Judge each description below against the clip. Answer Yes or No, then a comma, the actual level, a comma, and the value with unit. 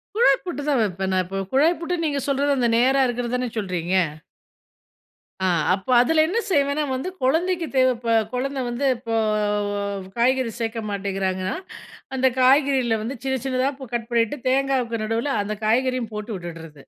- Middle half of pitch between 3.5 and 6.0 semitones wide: Yes, average, 4.2 semitones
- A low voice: No, very high, 250 Hz